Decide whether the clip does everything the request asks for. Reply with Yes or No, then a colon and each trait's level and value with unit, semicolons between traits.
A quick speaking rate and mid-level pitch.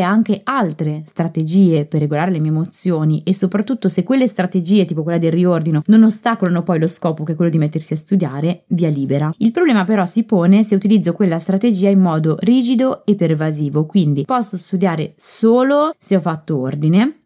Yes: fast, 185 wpm; medium, 180 Hz